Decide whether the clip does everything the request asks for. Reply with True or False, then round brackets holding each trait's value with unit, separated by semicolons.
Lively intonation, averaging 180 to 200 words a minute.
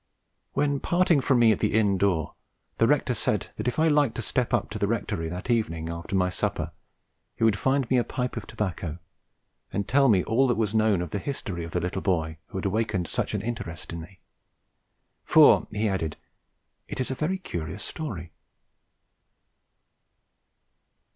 True (6.0 semitones; 185 wpm)